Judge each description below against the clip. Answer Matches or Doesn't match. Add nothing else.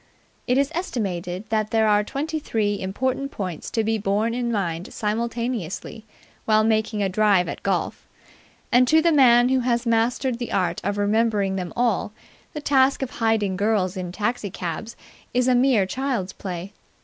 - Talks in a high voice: Matches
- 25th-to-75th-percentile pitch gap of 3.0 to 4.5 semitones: Matches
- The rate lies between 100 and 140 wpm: Doesn't match